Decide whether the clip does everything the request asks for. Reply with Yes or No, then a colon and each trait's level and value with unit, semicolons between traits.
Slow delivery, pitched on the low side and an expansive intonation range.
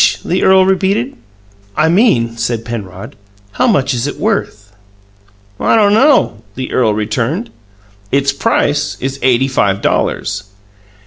Yes: slow, 130 wpm; low, 130 Hz; wide, 8.7 semitones